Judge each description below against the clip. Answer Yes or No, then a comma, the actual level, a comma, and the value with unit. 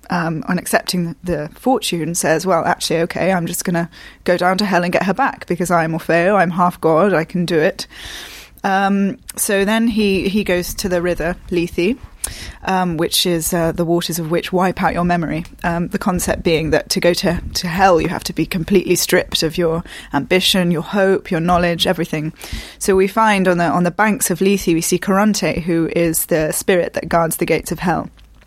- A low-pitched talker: No, medium, 175 Hz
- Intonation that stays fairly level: Yes, narrow, 2.3 semitones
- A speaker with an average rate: No, fast, 210 wpm